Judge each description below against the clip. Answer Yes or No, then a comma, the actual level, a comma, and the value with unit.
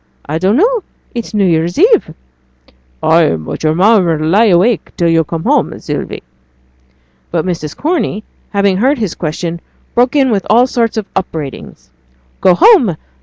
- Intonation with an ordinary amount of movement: No, wide, 6.2 semitones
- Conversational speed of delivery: Yes, average, 160 wpm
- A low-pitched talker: No, high, 190 Hz